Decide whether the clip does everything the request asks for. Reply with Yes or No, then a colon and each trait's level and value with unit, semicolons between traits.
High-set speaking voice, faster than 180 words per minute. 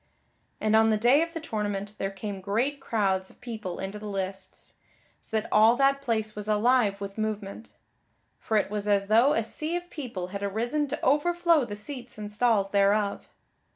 Yes: high, 215 Hz; average, 190 wpm